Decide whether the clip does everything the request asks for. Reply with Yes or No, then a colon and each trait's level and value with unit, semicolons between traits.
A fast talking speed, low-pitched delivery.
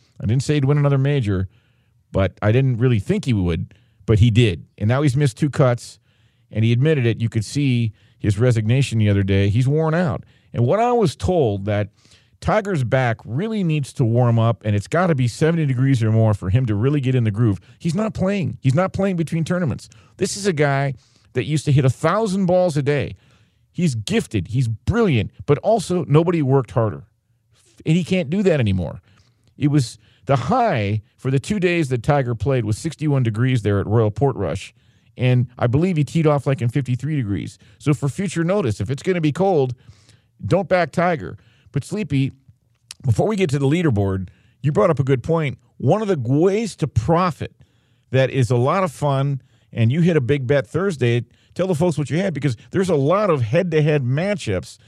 Yes: fast, 210 wpm; low, 130 Hz